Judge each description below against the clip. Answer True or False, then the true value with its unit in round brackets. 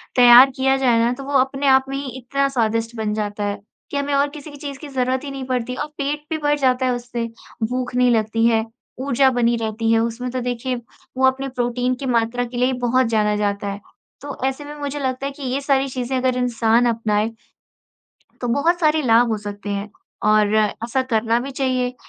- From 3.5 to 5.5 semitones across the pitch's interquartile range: False (3.0 semitones)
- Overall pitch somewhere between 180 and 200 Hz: False (250 Hz)